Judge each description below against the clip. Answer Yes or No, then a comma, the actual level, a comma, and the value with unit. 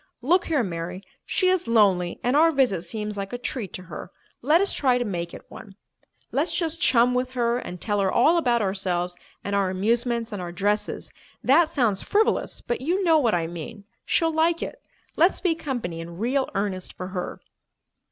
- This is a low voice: No, high, 230 Hz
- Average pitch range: No, wide, 7.3 semitones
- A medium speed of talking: Yes, average, 195 wpm